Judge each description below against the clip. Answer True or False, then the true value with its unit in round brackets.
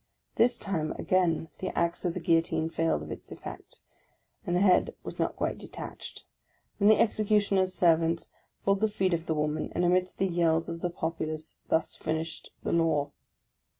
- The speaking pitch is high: False (170 Hz)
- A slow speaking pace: False (175 wpm)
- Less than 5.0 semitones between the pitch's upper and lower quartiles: True (2.5 semitones)